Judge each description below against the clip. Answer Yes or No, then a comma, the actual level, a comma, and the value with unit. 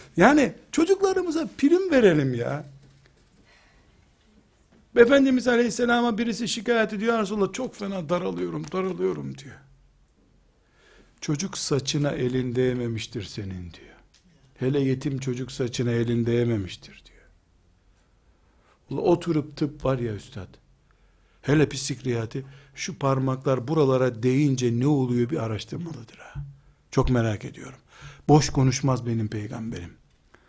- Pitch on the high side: No, low, 135 Hz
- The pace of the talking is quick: No, average, 105 wpm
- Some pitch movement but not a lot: No, wide, 6.7 semitones